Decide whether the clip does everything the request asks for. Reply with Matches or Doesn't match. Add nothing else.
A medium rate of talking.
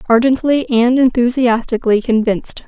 Doesn't match